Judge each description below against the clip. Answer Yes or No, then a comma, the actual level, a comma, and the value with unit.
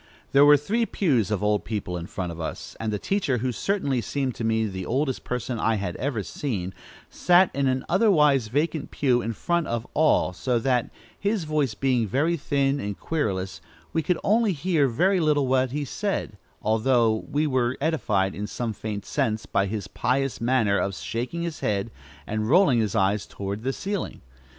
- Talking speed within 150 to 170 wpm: No, average, 185 wpm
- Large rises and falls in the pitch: Yes, wide, 5.7 semitones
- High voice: No, low, 125 Hz